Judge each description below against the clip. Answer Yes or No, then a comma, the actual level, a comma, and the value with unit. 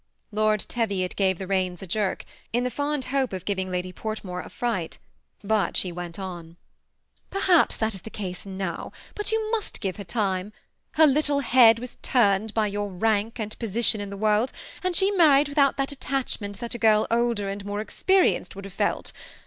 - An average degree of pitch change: Yes, average, 4.7 semitones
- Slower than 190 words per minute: No, average, 195 wpm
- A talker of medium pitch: No, high, 215 Hz